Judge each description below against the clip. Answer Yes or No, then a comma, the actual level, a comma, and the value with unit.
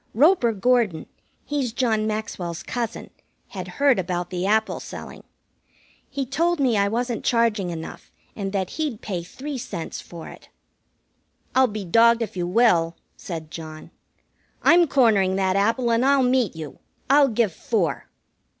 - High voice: Yes, high, 220 Hz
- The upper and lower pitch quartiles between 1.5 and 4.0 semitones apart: No, wide, 5.5 semitones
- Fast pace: No, average, 150 wpm